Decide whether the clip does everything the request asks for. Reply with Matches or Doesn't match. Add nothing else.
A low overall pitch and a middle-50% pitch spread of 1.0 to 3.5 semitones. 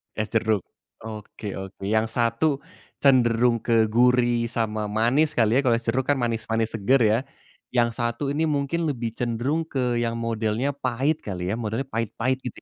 Matches